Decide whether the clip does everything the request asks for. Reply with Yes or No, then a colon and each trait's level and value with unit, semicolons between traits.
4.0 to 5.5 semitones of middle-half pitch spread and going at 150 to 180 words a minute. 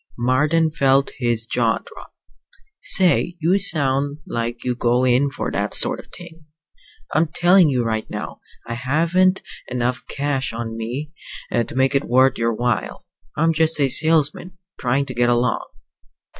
Yes: average, 4.7 semitones; average, 155 wpm